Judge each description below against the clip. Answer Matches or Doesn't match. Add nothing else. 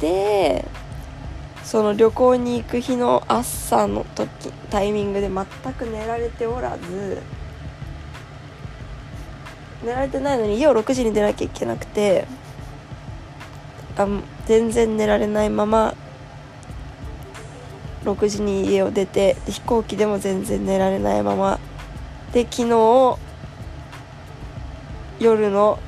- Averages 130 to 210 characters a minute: Matches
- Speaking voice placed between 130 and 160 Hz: Doesn't match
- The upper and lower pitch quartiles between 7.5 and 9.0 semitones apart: Matches